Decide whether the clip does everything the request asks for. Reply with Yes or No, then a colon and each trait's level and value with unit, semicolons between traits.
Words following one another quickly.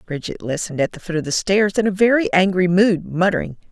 Yes: fast, 225 wpm